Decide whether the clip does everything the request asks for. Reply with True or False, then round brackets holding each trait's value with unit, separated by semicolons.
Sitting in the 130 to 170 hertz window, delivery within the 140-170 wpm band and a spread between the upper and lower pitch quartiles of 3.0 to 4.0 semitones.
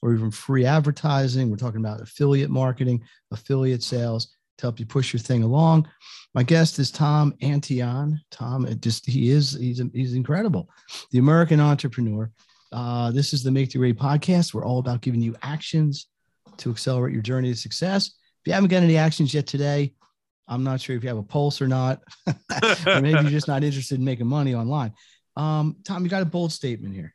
False (135 Hz; 200 wpm; 3.5 semitones)